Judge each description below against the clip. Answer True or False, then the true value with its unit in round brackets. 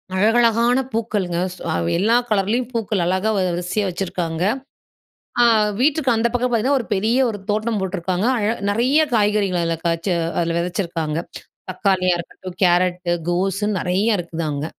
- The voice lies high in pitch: True (195 Hz)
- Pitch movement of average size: True (4.2 semitones)